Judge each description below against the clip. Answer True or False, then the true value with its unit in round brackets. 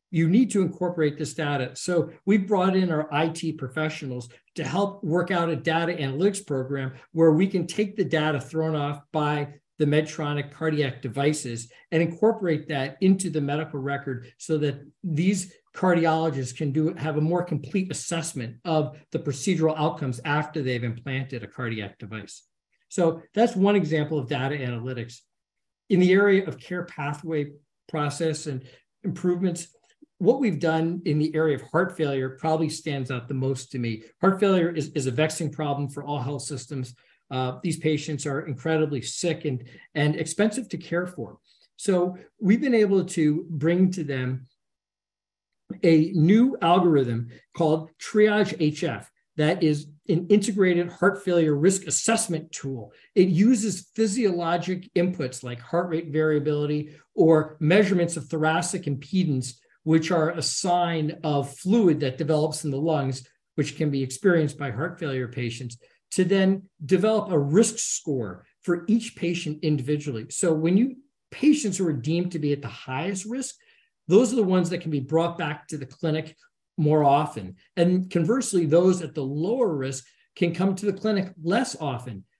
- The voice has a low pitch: False (160 Hz)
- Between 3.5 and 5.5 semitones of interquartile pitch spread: True (4.0 semitones)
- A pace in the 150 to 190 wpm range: True (160 wpm)